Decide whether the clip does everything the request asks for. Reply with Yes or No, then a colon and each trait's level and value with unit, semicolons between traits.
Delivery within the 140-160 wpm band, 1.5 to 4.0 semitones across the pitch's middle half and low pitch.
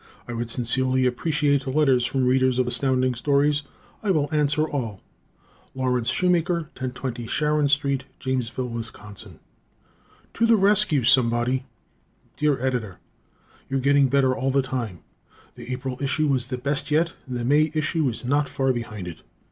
Yes: average, 150 wpm; average, 2.8 semitones; low, 130 Hz